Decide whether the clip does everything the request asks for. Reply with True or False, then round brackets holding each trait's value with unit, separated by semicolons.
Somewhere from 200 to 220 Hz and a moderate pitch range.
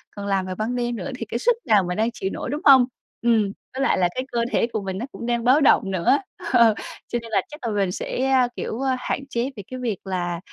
False (235 Hz; 4.4 semitones)